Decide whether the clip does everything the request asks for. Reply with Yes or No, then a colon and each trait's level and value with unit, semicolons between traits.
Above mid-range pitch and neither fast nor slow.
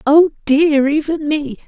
Yes: very high, 295 Hz; average, 145 wpm